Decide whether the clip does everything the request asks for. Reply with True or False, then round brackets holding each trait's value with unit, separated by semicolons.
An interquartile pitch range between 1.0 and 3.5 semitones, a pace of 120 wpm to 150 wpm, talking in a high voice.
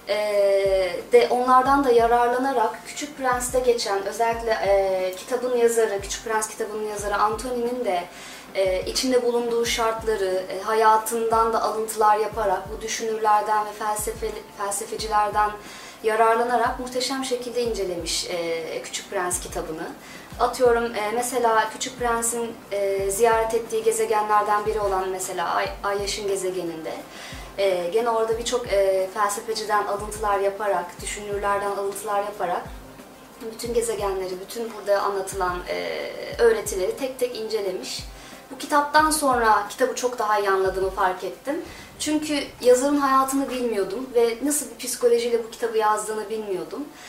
True (3.2 semitones; 125 wpm; 220 Hz)